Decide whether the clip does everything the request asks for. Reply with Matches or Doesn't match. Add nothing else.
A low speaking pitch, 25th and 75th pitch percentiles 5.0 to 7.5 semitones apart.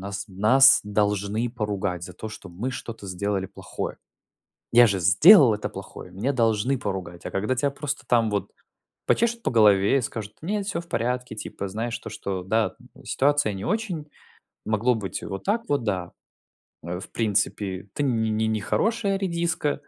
Matches